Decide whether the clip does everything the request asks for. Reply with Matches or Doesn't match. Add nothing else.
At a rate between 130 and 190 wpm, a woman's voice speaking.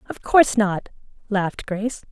Matches